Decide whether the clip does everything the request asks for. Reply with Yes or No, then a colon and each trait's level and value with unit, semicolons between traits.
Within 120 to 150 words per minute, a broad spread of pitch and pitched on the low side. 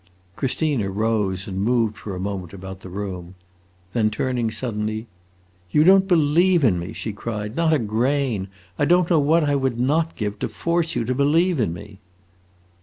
No: average, 180 wpm; wide, 6.6 semitones; low, 115 Hz